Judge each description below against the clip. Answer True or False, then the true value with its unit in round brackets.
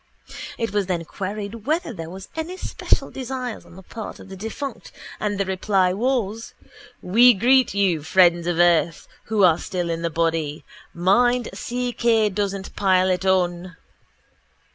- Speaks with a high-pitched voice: True (195 Hz)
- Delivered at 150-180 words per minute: True (160 wpm)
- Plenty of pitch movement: False (4.6 semitones)